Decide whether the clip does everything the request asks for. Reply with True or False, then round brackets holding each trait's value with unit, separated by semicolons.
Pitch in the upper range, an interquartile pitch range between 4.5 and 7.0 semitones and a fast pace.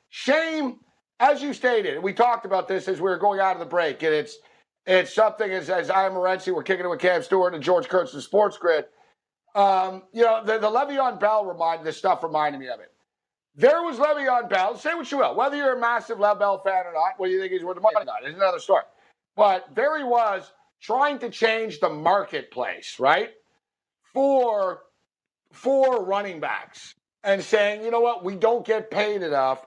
True (210 Hz; 5.2 semitones; 210 wpm)